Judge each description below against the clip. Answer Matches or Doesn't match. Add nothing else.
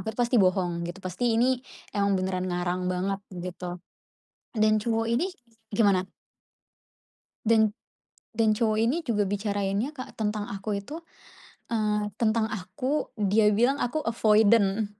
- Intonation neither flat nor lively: Matches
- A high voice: Matches